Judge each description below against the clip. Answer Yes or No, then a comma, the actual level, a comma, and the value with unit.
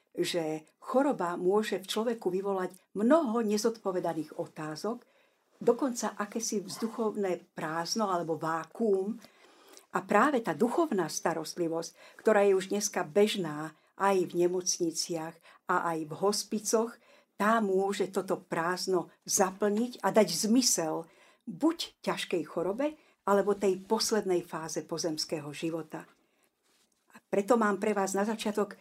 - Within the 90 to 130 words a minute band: Yes, average, 115 wpm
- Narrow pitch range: No, average, 4.4 semitones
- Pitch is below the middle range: No, high, 195 Hz